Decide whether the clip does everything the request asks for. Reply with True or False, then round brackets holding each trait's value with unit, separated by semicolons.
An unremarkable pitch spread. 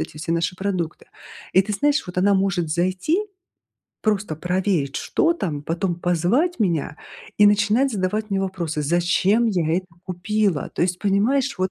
True (3.3 semitones)